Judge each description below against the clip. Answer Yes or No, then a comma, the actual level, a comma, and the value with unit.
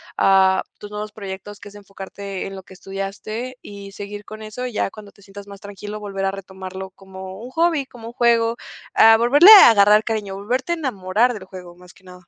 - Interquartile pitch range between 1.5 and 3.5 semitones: Yes, narrow, 2.6 semitones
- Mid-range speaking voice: No, high, 205 Hz